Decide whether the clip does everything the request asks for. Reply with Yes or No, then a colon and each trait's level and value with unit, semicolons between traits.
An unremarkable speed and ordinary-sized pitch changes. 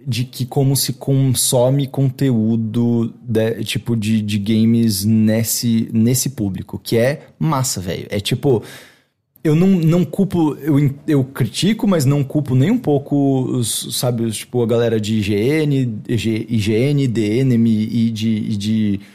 Yes: average, 145 wpm; average, 3.8 semitones